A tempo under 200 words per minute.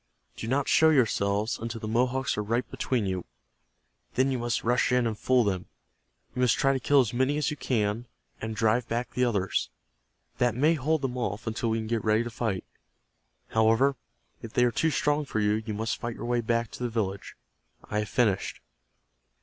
No: fast, 205 wpm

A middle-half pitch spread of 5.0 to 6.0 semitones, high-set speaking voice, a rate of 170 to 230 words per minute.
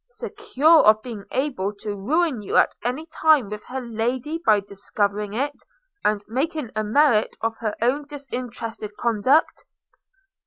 No: wide, 5.5 semitones; high, 240 Hz; average, 145 wpm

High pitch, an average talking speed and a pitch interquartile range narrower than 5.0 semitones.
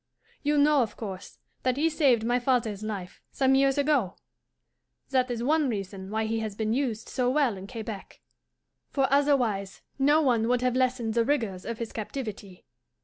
Yes: high, 240 Hz; average, 175 wpm; average, 4.0 semitones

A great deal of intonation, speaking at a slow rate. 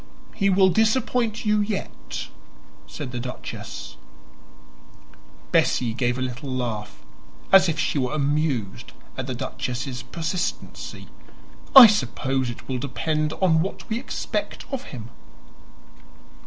Yes: wide, 7.6 semitones; slow, 120 wpm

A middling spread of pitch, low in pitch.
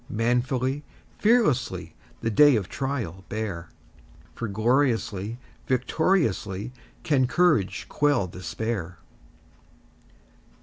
No: wide, 5.9 semitones; low, 120 Hz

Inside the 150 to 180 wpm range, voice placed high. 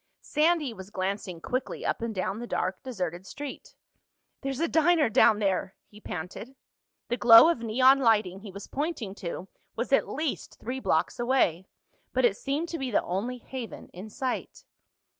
Yes: average, 170 wpm; high, 230 Hz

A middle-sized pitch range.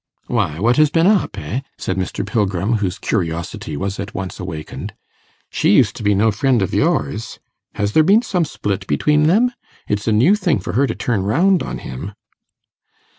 No: wide, 7.9 semitones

